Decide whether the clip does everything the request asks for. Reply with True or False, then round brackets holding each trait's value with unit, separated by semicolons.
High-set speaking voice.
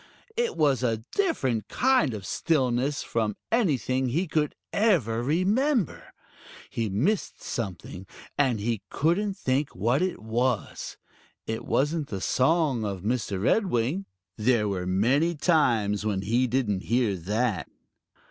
False (125 Hz)